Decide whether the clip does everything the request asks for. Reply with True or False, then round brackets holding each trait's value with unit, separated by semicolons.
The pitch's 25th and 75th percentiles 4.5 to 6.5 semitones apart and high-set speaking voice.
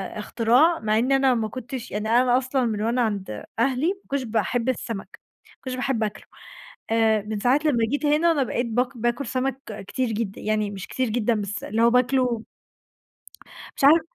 False (3.3 semitones; 240 Hz)